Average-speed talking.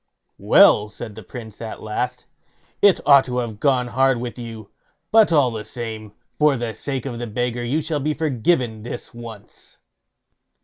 Yes: average, 170 wpm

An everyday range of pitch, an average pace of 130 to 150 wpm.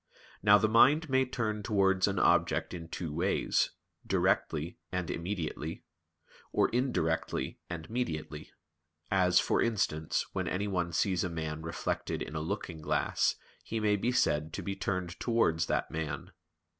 Yes: average, 4.7 semitones; average, 145 wpm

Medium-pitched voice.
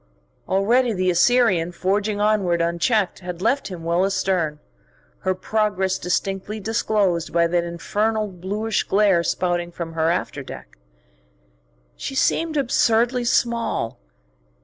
No: high, 195 Hz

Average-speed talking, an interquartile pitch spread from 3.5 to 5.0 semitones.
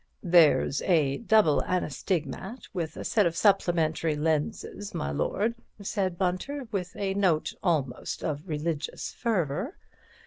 No: slow, 125 wpm; average, 4.5 semitones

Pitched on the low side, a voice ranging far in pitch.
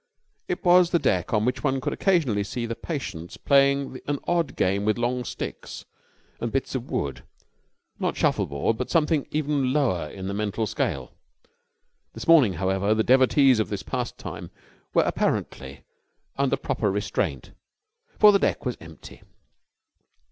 Yes: low, 125 Hz; wide, 5.8 semitones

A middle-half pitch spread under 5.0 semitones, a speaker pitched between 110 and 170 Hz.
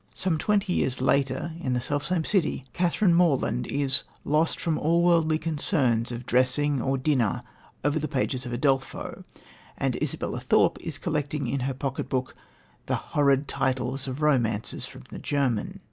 Yes: average, 3.4 semitones; medium, 140 Hz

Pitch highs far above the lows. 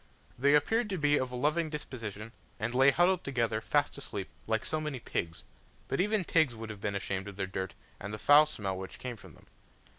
Yes: wide, 6.3 semitones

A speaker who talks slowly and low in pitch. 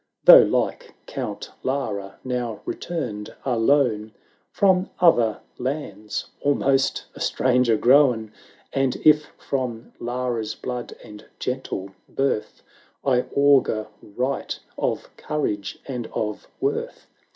Yes: slow, 105 wpm; low, 125 Hz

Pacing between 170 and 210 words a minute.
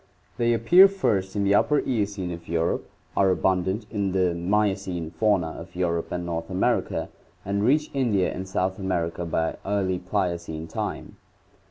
No: average, 155 wpm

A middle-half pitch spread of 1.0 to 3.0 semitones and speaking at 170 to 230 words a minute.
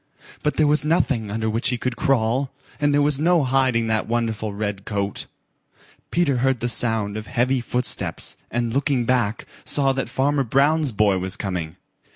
No: average, 4.0 semitones; average, 175 wpm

